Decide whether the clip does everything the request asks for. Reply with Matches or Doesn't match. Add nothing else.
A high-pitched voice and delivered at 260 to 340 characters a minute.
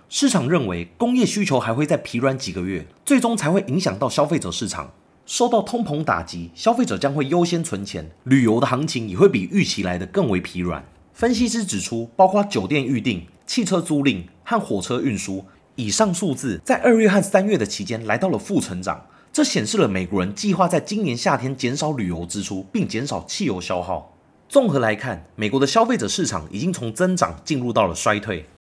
Doesn't match